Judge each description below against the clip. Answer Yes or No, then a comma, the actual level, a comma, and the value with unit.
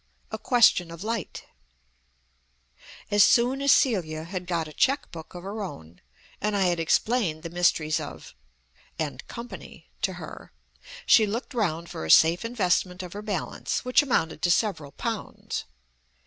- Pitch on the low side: No, medium, 185 Hz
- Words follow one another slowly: No, average, 160 wpm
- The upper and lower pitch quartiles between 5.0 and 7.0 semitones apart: Yes, wide, 5.6 semitones